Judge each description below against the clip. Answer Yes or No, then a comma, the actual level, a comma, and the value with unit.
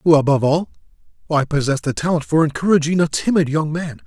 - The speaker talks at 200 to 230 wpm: No, average, 175 wpm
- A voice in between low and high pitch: Yes, medium, 150 Hz